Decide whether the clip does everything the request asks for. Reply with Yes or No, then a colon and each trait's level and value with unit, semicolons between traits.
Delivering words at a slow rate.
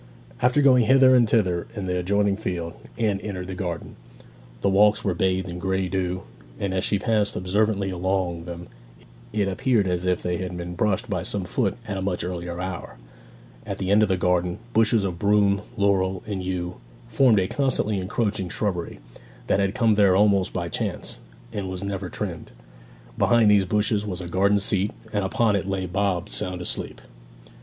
No: average, 185 wpm